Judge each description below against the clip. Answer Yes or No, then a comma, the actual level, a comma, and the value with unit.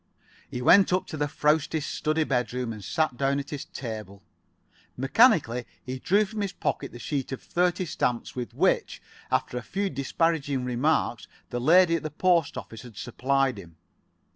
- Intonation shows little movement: No, average, 5.0 semitones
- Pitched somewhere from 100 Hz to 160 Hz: Yes, medium, 140 Hz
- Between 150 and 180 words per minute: Yes, average, 175 wpm